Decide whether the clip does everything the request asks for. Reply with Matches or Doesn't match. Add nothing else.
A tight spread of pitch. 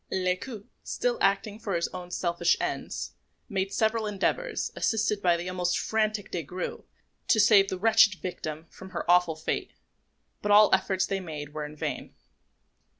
Doesn't match